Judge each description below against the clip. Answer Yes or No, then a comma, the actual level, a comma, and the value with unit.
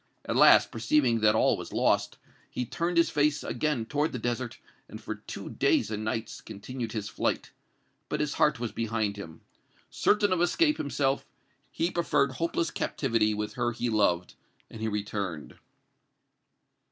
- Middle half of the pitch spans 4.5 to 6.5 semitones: Yes, wide, 5.5 semitones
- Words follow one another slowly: No, average, 160 wpm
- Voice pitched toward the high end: No, low, 115 Hz